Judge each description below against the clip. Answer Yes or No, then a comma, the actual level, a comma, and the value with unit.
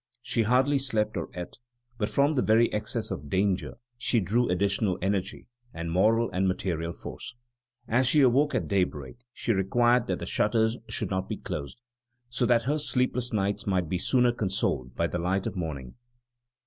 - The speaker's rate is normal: Yes, average, 175 wpm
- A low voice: Yes, low, 105 Hz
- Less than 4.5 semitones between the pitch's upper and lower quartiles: No, average, 4.8 semitones